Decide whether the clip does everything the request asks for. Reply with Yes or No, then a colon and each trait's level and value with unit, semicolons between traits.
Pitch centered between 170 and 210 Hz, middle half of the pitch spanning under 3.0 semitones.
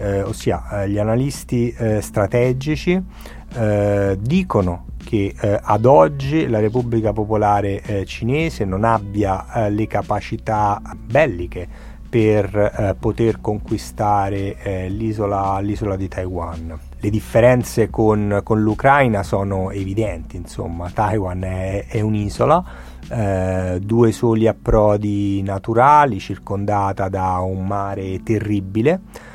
No: low, 105 Hz; narrow, 2.5 semitones